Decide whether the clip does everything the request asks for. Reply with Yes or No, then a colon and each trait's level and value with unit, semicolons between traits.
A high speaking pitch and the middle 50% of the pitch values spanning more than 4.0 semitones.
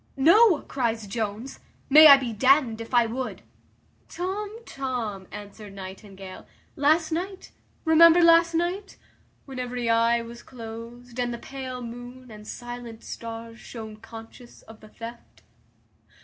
No: high, 240 Hz; average, 3.5 semitones